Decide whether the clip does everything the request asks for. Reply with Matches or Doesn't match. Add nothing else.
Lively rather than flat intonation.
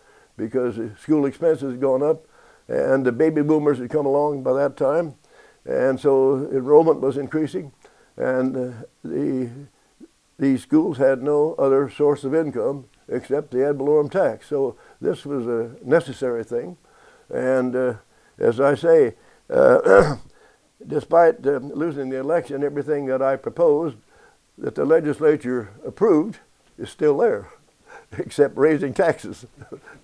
Doesn't match